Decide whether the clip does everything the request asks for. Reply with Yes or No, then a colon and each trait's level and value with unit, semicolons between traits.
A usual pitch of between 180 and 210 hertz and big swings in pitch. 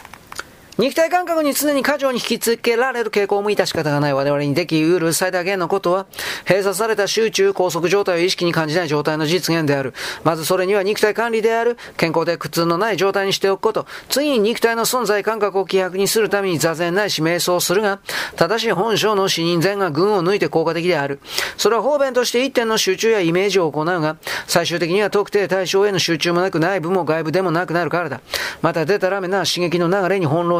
No: high, 190 Hz; average, 3.6 semitones